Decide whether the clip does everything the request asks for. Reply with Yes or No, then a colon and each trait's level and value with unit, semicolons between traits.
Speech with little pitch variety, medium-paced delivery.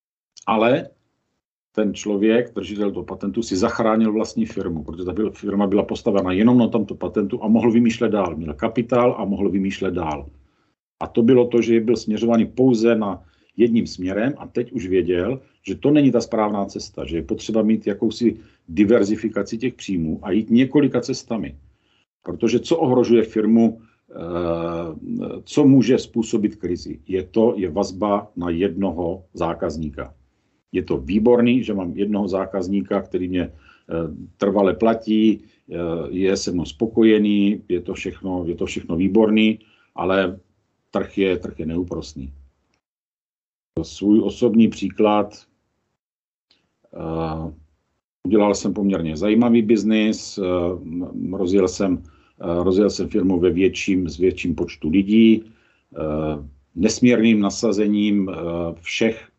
No: average, 3.8 semitones; average, 130 wpm